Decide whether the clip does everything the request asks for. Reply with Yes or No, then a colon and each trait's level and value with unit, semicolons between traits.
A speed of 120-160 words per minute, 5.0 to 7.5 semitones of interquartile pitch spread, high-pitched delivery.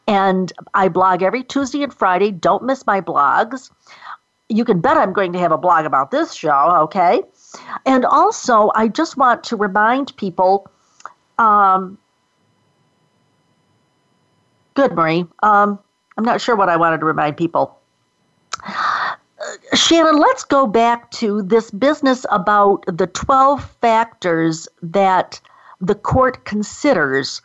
Yes: slow, 135 wpm; wide, 5.4 semitones; high, 210 Hz